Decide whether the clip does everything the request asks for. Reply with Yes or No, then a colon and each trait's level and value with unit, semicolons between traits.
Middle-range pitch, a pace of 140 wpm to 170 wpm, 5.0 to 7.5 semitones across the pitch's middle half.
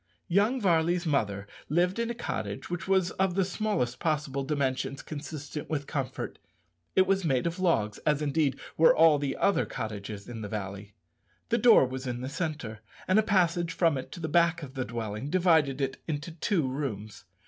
No: medium, 150 Hz; average, 185 wpm; wide, 5.4 semitones